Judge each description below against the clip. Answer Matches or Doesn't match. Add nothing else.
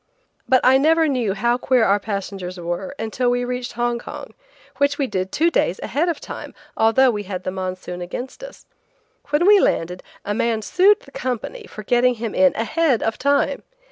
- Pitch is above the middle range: Matches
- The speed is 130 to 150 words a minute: Doesn't match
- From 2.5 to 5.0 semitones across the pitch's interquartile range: Doesn't match